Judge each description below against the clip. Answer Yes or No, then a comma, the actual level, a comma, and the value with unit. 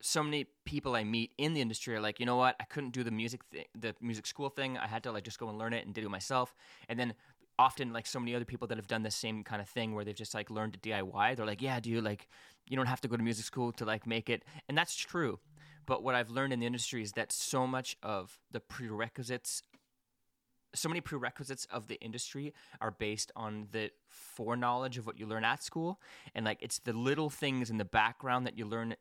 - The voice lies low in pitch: Yes, low, 120 Hz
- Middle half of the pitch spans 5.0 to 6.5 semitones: No, average, 2.9 semitones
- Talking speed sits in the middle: No, fast, 255 wpm